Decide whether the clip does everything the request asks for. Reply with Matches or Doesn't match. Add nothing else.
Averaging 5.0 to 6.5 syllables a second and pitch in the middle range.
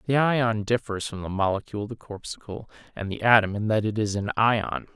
Doesn't match